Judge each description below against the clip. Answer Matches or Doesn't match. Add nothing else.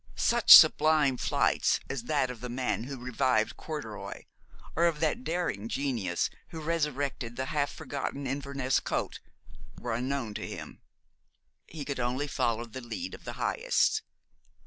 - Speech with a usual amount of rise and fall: Matches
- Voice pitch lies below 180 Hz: Matches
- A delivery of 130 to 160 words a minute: Matches